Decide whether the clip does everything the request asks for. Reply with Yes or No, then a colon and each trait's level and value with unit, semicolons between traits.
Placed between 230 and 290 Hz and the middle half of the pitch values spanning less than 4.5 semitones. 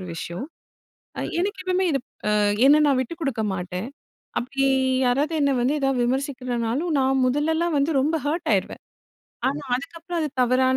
Yes: very high, 275 Hz; average, 4.1 semitones